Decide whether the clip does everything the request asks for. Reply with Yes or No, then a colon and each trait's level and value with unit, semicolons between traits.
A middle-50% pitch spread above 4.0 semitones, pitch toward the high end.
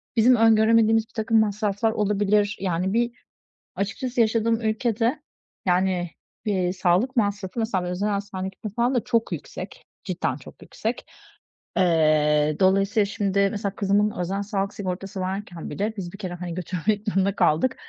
No: average, 2.8 semitones; high, 200 Hz